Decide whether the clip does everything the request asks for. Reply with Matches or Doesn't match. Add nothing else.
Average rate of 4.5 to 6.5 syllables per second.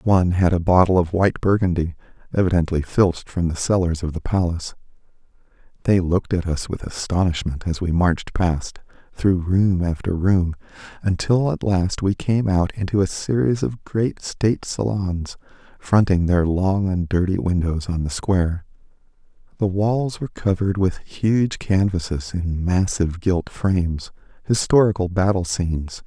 Matches